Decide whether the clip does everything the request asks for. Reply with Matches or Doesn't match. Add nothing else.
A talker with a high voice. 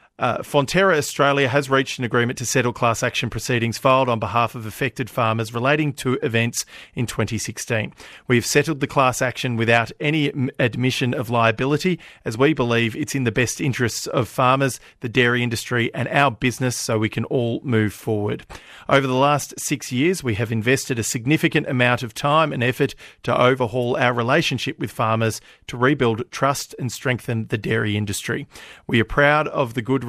Doesn't match